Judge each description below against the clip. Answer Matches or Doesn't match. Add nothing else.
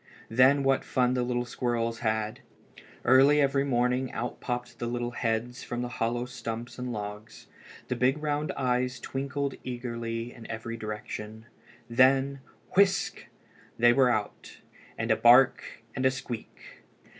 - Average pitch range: Doesn't match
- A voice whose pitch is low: Matches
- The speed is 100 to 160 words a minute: Matches